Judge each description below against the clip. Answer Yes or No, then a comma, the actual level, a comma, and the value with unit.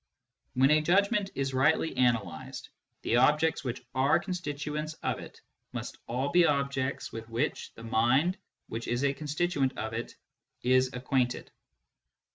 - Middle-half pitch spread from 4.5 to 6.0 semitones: No, average, 3.7 semitones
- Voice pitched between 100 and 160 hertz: Yes, low, 135 Hz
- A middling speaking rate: Yes, average, 145 wpm